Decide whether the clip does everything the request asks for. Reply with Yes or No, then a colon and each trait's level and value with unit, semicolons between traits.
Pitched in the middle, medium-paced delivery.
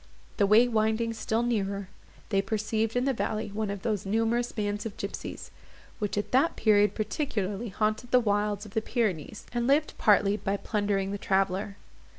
No: high, 215 Hz; average, 170 wpm